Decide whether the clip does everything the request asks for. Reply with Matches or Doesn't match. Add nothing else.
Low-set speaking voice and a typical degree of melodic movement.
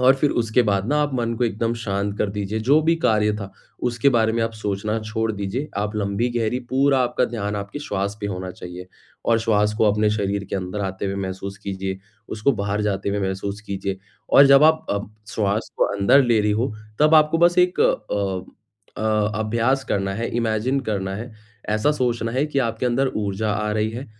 Matches